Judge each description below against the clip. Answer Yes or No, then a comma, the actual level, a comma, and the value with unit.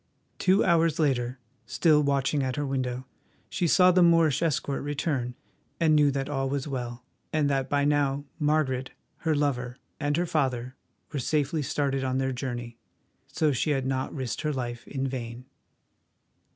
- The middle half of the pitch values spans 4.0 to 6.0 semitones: No, narrow, 2.6 semitones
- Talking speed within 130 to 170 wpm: Yes, average, 165 wpm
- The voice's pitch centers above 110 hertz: Yes, medium, 140 Hz